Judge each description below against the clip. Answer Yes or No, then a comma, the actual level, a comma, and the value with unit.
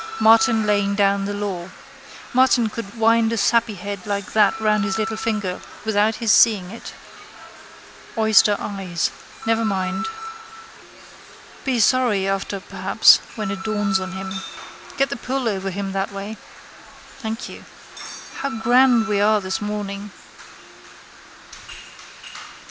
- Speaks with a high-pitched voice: Yes, high, 210 Hz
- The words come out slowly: Yes, slow, 125 wpm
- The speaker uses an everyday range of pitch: No, narrow, 2.3 semitones